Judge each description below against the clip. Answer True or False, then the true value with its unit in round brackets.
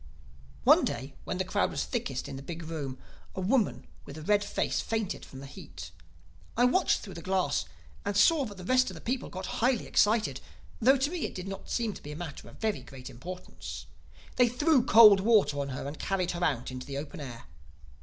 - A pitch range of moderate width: False (7.6 semitones)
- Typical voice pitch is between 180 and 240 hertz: True (190 Hz)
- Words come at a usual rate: False (215 wpm)